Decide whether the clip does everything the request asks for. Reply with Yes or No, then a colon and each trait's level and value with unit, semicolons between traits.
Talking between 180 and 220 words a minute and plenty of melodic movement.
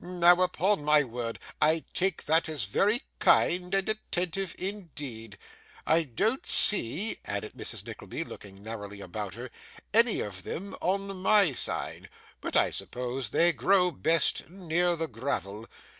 No: average, 145 wpm; wide, 8.4 semitones